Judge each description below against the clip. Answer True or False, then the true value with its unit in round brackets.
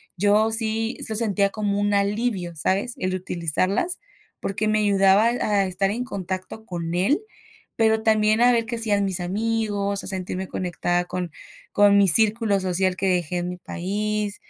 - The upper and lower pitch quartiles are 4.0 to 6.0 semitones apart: False (2.9 semitones)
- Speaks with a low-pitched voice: False (200 Hz)